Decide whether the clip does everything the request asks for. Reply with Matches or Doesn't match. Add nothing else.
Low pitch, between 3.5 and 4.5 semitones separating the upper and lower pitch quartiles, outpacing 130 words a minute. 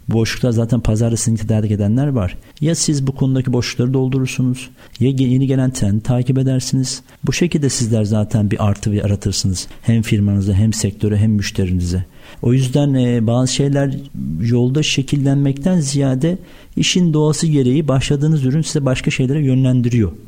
Matches